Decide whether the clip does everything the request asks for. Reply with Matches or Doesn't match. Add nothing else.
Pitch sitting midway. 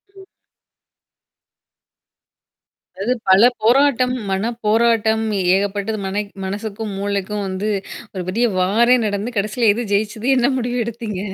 Doesn't match